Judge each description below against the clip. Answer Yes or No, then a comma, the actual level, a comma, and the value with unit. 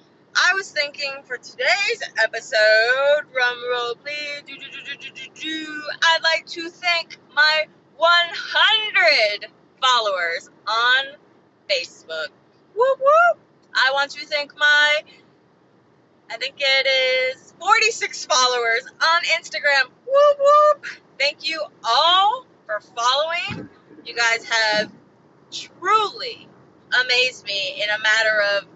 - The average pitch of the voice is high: Yes, very high, 290 Hz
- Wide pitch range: No, average, 4.9 semitones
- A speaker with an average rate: No, slow, 120 wpm